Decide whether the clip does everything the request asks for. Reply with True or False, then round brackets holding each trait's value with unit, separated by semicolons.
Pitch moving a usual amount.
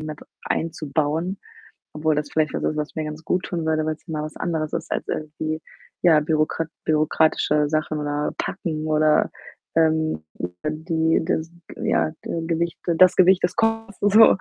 False (1.5 semitones)